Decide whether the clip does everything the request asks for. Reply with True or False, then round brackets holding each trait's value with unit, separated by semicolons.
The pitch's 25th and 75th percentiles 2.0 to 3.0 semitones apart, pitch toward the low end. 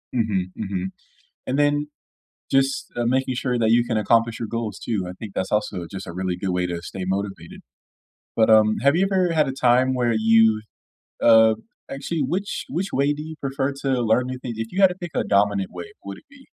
False (5.1 semitones; 115 Hz)